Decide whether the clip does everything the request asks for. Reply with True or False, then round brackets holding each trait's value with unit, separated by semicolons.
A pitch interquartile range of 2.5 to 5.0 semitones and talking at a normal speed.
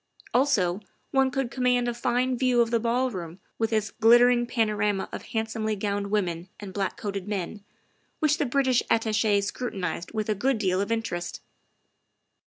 True (3.5 semitones; 160 wpm)